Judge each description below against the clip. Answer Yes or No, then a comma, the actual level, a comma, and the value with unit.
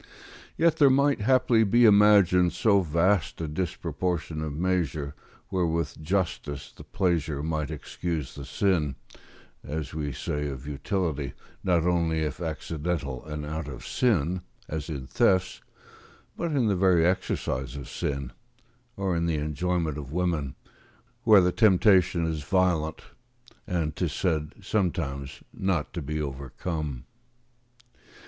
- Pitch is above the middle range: No, very low, 80 Hz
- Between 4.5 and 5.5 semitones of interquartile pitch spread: No, average, 3.9 semitones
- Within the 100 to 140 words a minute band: Yes, slow, 135 wpm